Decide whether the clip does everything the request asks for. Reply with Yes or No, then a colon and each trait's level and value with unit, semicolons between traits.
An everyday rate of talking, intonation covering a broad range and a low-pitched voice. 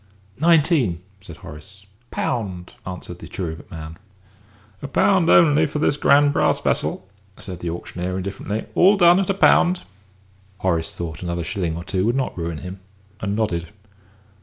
Yes: average, 160 wpm; wide, 8.9 semitones; very low, 95 Hz